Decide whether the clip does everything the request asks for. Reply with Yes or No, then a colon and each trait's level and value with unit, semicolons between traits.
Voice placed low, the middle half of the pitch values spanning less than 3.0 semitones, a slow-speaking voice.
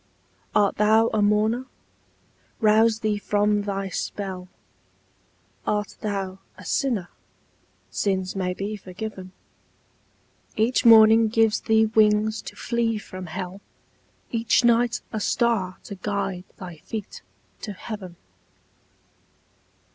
No: high, 210 Hz; narrow, 2.4 semitones; slow, 110 wpm